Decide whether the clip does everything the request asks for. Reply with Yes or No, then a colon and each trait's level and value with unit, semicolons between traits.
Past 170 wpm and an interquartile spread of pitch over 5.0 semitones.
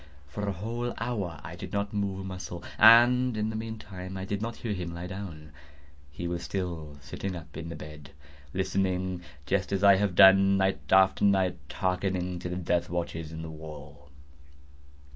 No: average, 180 wpm; average, 2.9 semitones